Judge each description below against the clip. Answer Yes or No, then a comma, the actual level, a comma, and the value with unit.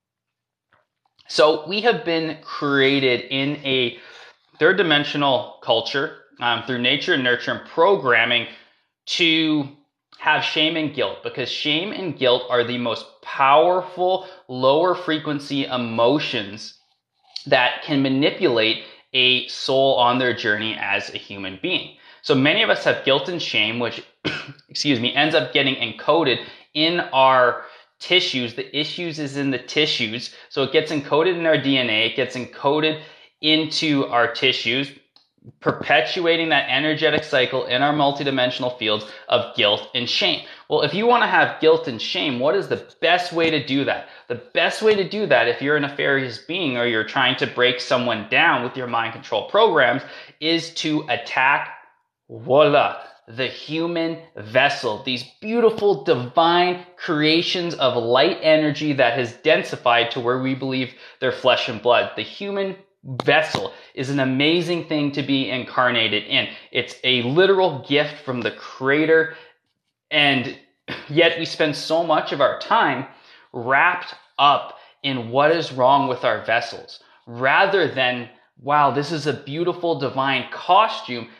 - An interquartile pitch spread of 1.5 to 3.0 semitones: No, average, 4.3 semitones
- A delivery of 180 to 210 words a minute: No, average, 150 wpm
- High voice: No, medium, 140 Hz